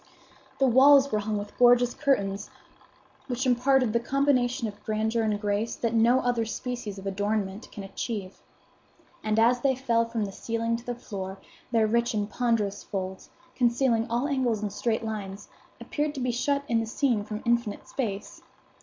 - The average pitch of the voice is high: Yes, high, 230 Hz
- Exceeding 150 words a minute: Yes, average, 170 wpm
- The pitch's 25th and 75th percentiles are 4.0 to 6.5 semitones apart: No, average, 2.9 semitones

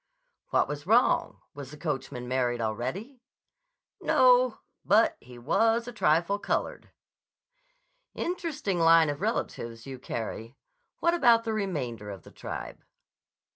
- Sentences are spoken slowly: Yes, slow, 125 wpm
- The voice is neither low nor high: Yes, medium, 165 Hz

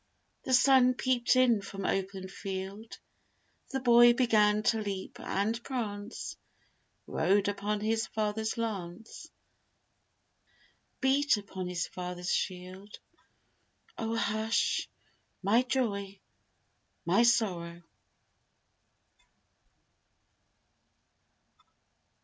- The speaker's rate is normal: No, slow, 80 wpm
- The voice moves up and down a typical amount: Yes, average, 3.5 semitones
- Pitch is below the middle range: No, high, 210 Hz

